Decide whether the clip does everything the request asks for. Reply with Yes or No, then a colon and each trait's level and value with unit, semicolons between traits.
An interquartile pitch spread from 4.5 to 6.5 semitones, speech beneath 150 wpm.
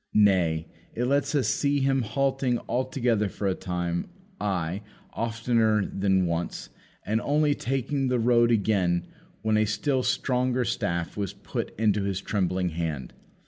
Yes: wide, 5.4 semitones; average, 140 wpm